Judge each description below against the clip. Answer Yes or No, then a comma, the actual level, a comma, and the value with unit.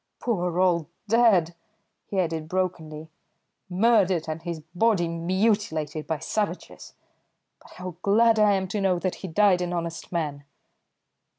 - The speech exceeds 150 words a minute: No, slow, 135 wpm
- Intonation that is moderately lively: Yes, average, 3.5 semitones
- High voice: No, medium, 180 Hz